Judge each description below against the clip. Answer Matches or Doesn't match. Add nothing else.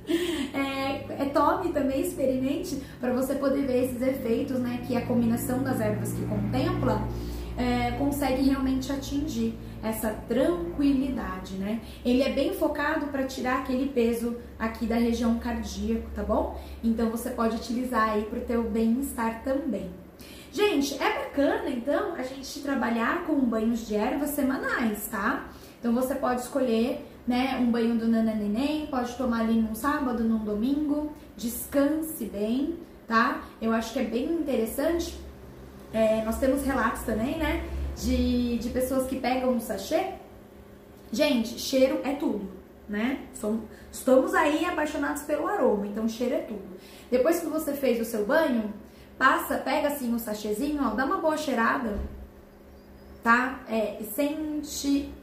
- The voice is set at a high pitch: Matches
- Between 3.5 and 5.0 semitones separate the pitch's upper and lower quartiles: Matches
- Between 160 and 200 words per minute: Doesn't match